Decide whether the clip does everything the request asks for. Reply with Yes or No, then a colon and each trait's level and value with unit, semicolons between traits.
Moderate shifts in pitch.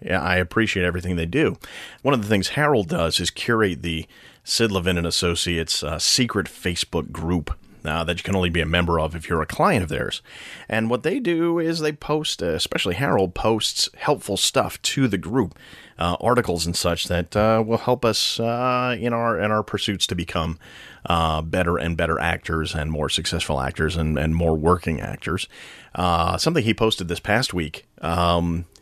Yes: average, 5.0 semitones